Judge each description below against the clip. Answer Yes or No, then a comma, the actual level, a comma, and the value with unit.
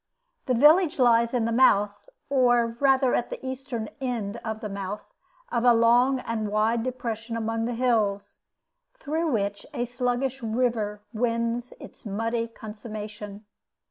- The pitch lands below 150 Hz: No, high, 230 Hz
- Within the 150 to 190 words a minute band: No, average, 140 wpm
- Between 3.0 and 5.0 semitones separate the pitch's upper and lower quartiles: No, narrow, 2.5 semitones